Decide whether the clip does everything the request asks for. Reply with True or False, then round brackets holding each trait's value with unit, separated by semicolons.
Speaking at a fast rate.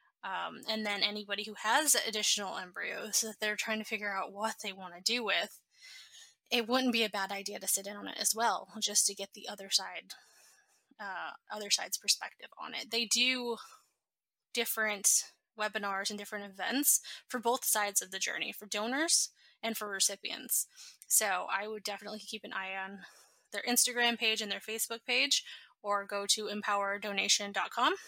False (175 wpm)